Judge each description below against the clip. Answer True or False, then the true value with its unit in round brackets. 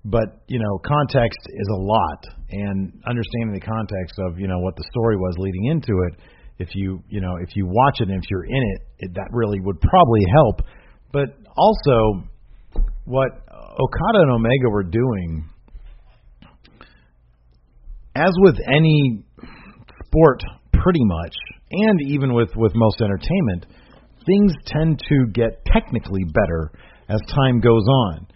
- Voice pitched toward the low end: True (110 Hz)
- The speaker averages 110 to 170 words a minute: True (150 wpm)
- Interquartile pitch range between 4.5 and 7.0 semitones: True (5.5 semitones)